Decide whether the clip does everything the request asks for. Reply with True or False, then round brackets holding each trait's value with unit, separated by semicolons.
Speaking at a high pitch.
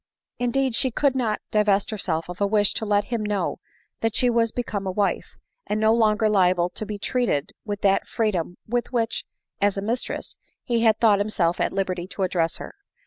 True (210 Hz)